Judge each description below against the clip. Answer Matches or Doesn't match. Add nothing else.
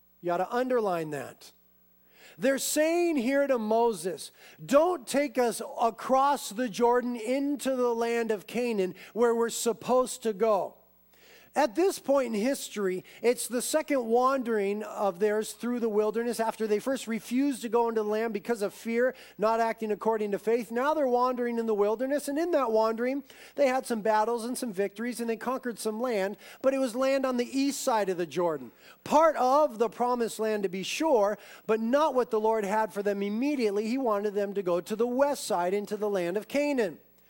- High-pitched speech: Matches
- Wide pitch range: Doesn't match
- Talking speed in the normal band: Matches